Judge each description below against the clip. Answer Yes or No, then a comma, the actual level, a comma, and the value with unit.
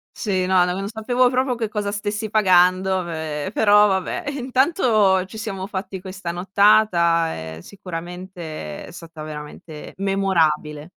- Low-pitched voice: No, high, 190 Hz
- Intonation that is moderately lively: Yes, average, 3.4 semitones